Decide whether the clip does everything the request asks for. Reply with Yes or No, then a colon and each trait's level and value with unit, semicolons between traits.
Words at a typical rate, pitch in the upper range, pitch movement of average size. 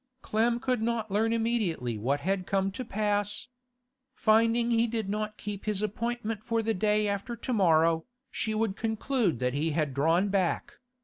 Yes: average, 170 wpm; high, 210 Hz; average, 3.4 semitones